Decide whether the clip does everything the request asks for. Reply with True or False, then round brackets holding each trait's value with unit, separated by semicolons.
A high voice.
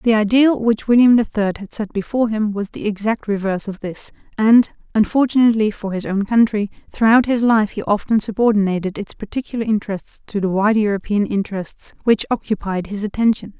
True (215 Hz)